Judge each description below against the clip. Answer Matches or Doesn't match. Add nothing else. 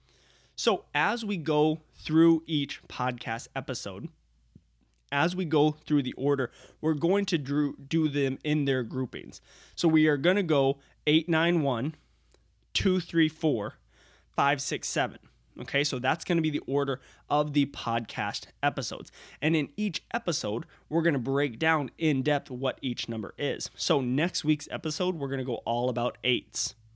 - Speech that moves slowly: Doesn't match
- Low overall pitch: Doesn't match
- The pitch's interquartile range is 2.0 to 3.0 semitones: Doesn't match